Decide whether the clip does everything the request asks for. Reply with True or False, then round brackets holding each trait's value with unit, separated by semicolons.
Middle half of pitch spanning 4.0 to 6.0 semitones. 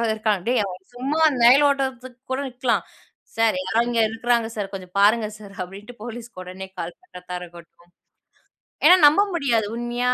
True (4.3 semitones)